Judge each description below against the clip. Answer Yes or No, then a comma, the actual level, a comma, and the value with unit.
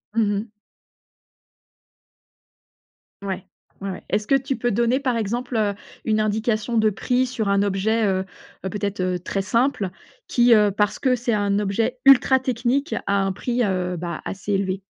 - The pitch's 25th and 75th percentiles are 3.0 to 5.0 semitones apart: Yes, average, 3.5 semitones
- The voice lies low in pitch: No, high, 215 Hz